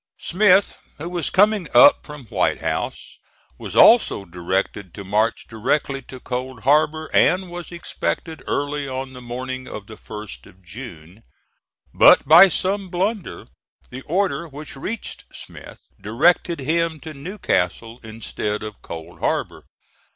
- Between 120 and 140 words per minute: Yes, slow, 135 wpm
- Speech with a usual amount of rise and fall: No, wide, 7.7 semitones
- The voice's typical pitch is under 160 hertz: Yes, low, 135 Hz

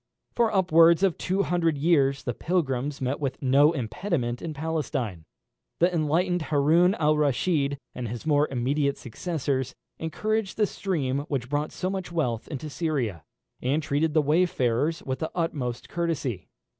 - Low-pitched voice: No, medium, 150 Hz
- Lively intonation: No, average, 4.3 semitones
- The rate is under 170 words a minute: Yes, average, 150 wpm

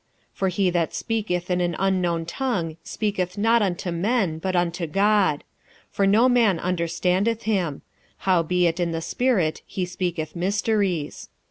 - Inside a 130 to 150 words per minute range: Yes, average, 145 wpm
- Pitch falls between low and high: Yes, medium, 180 Hz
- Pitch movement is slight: No, average, 3.2 semitones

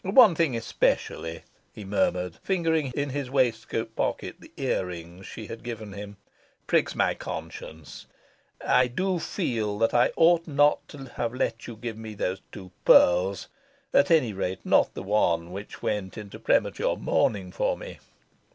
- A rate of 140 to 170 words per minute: Yes, average, 160 wpm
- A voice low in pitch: Yes, low, 110 Hz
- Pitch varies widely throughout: Yes, wide, 6.2 semitones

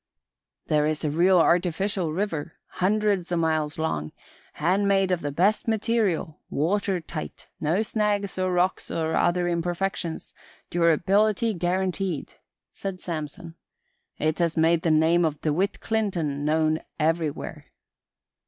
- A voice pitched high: No, medium, 175 Hz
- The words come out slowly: Yes, slow, 125 wpm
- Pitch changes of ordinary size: Yes, average, 3.5 semitones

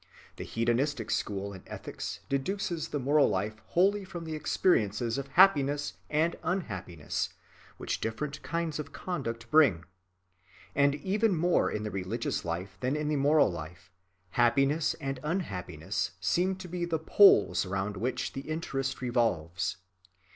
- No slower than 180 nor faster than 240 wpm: No, average, 140 wpm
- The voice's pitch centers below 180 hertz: Yes, low, 135 Hz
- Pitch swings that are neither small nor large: No, wide, 7.5 semitones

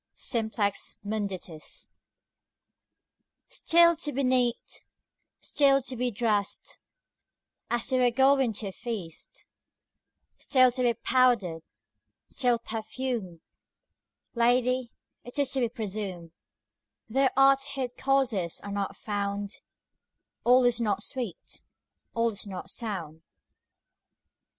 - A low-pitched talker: No, high, 235 Hz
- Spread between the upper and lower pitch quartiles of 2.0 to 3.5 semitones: No, average, 4.1 semitones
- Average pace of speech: No, slow, 110 wpm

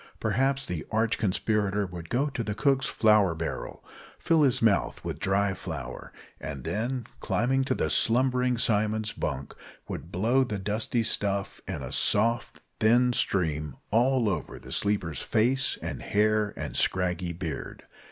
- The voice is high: No, low, 105 Hz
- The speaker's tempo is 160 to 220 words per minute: No, average, 150 wpm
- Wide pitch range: No, average, 4.6 semitones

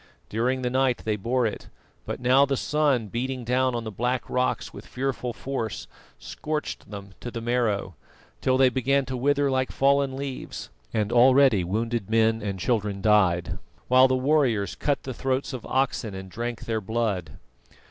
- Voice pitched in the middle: No, low, 125 Hz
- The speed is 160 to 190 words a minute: Yes, average, 170 wpm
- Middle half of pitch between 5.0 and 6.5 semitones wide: No, average, 3.2 semitones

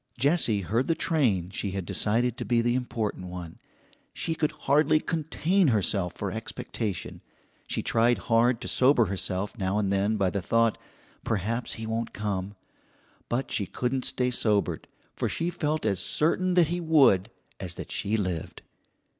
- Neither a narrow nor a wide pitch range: No, wide, 5.9 semitones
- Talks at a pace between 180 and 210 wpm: No, average, 165 wpm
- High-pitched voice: No, low, 115 Hz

